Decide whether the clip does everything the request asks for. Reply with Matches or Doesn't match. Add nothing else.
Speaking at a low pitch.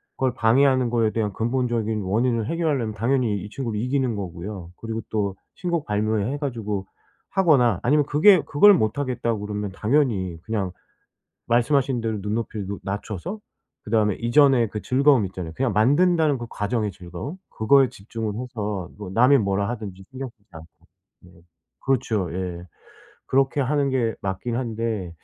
Matches